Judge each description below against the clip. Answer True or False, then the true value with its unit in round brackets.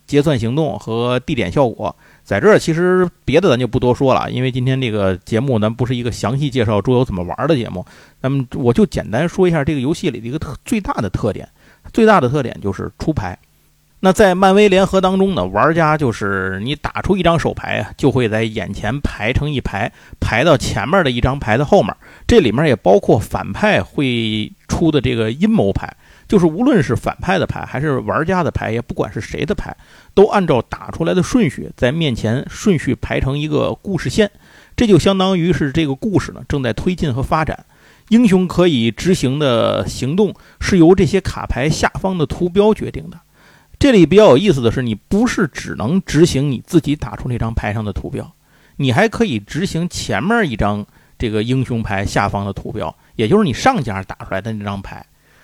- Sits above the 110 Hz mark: True (135 Hz)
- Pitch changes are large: True (8.0 semitones)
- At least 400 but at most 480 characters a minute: False (305 characters per minute)